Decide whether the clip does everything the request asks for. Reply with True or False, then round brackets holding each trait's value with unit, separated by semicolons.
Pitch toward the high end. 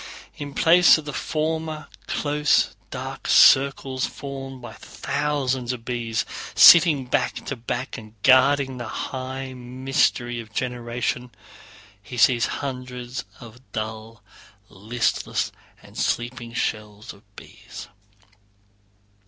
False (130 Hz)